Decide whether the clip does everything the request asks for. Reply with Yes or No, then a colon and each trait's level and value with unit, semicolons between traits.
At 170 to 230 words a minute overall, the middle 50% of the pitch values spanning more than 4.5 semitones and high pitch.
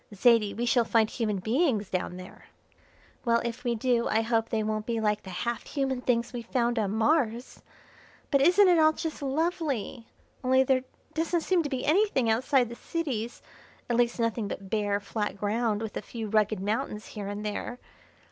No: average, 185 wpm; average, 3.7 semitones; high, 235 Hz